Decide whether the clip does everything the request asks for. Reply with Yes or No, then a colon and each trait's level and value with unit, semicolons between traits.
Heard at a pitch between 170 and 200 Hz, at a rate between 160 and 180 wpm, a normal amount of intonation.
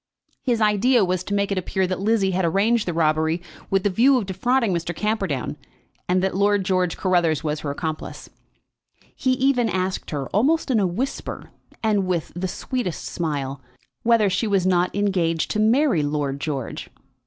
Yes: high, 190 Hz; average, 175 wpm; average, 4.3 semitones